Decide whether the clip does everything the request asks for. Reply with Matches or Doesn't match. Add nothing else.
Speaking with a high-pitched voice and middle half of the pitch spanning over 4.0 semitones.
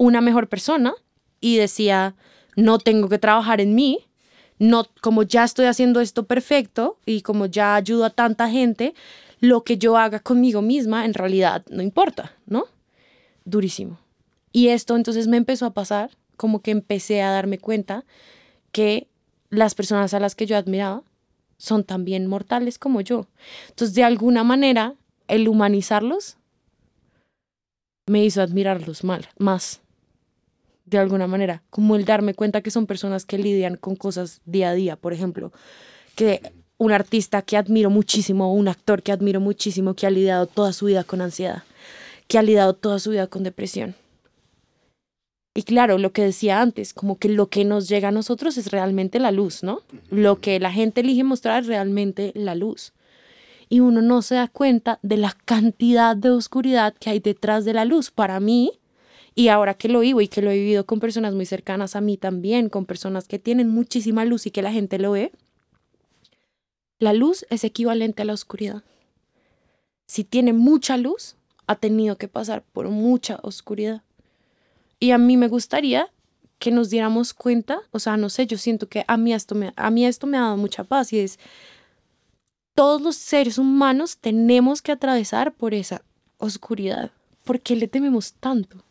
Doesn't match